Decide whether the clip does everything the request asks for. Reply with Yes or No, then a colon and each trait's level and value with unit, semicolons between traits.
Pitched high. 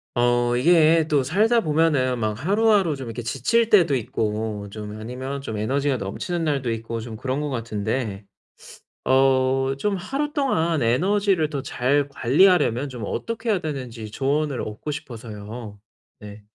No: low, 135 Hz